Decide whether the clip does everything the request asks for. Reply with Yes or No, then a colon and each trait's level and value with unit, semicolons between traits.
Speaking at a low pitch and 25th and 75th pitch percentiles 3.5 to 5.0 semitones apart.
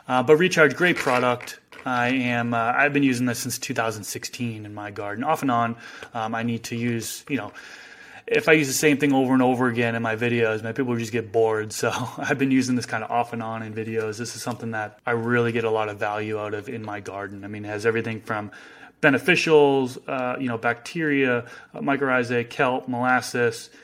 No: low, 120 Hz; narrow, 2.5 semitones